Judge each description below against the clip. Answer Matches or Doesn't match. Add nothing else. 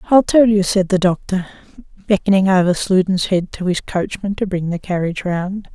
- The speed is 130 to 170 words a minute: Doesn't match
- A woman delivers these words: Matches